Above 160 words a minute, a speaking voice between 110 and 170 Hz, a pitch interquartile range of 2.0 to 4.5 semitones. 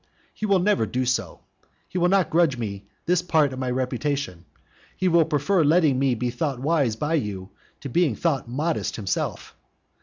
No: average, 180 wpm; medium, 140 Hz; average, 5.3 semitones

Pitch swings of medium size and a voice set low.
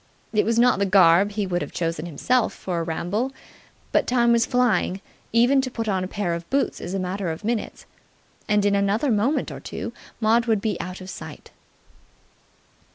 No: average, 4.3 semitones; high, 205 Hz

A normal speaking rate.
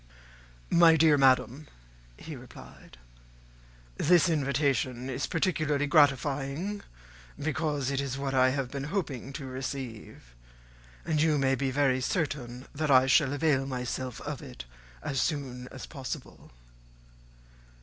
No: slow, 125 wpm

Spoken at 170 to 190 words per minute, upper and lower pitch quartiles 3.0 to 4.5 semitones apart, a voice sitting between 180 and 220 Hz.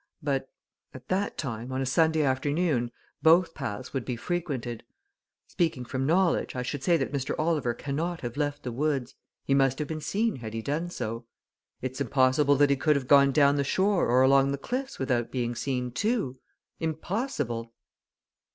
No: average, 180 wpm; average, 4.0 semitones; medium, 140 Hz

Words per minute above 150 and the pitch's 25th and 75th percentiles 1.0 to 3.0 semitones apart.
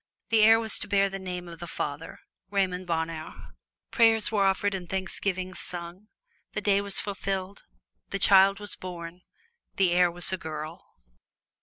Yes: average, 160 wpm; narrow, 2.4 semitones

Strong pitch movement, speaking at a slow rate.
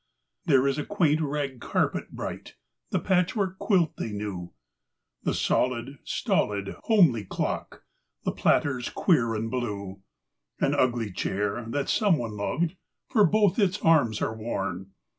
Yes: wide, 7.9 semitones; slow, 130 wpm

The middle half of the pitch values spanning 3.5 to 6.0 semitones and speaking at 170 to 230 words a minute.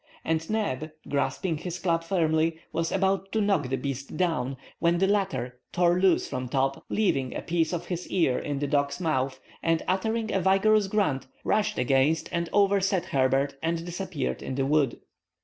Yes: wide, 5.6 semitones; average, 175 wpm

